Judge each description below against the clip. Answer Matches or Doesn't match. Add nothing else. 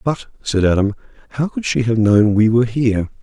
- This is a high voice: Doesn't match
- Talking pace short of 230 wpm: Matches